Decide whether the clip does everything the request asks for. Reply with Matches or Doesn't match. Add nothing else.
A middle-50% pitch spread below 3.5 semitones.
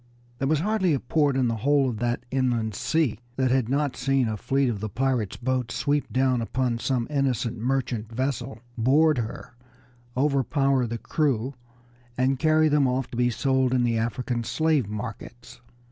Matches